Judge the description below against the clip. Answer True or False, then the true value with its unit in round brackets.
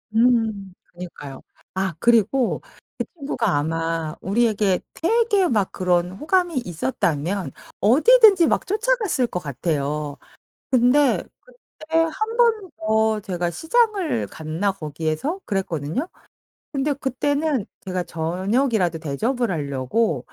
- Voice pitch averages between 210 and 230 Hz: True (215 Hz)